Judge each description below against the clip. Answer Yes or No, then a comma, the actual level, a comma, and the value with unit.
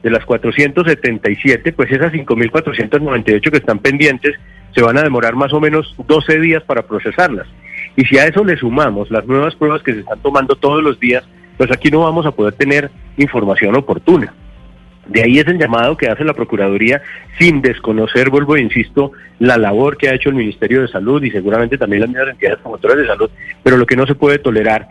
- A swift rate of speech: Yes, fast, 200 wpm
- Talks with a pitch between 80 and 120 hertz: No, low, 135 Hz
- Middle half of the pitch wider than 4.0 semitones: Yes, average, 4.6 semitones